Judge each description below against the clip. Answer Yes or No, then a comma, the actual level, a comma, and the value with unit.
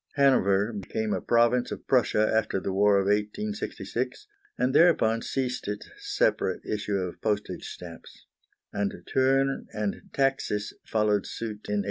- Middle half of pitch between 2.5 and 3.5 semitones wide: No, average, 4.0 semitones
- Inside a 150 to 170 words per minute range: No, average, 140 wpm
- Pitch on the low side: Yes, low, 110 Hz